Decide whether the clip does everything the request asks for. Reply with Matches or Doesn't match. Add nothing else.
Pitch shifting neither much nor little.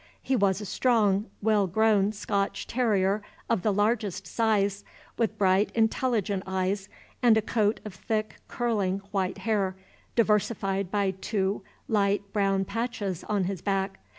Doesn't match